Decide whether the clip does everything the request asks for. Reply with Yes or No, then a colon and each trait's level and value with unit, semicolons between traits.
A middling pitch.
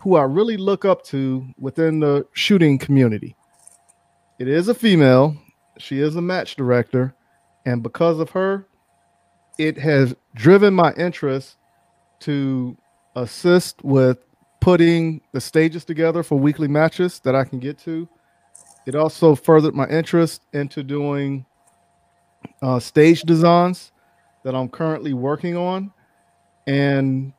Yes: medium, 150 Hz